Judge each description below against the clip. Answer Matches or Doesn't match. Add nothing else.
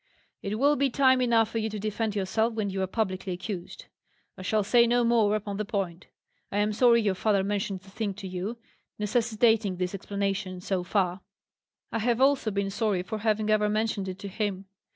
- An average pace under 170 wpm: Doesn't match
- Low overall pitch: Doesn't match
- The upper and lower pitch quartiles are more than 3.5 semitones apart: Doesn't match